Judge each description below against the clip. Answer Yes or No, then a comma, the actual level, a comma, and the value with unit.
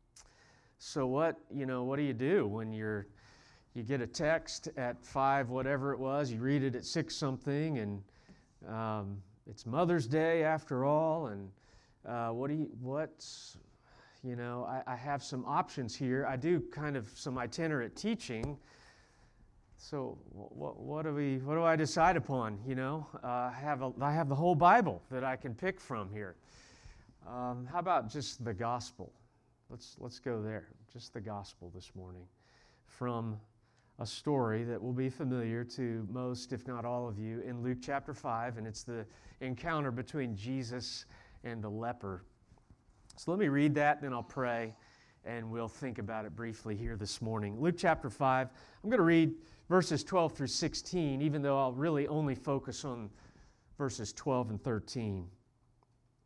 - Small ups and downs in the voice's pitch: No, average, 3.9 semitones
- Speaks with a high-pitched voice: No, low, 125 Hz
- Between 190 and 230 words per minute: No, average, 175 wpm